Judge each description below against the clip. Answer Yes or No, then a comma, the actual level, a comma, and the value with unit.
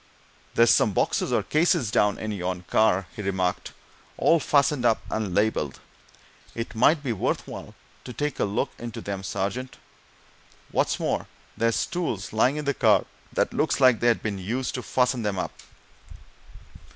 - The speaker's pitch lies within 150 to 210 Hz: No, low, 115 Hz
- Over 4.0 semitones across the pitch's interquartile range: Yes, average, 4.6 semitones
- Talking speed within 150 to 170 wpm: Yes, average, 165 wpm